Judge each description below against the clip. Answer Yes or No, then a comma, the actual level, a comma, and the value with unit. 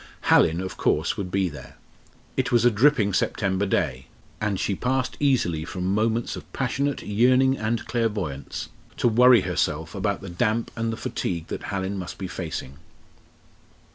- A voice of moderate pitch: No, low, 100 Hz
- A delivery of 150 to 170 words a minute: Yes, average, 160 wpm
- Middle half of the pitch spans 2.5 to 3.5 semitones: No, average, 4.6 semitones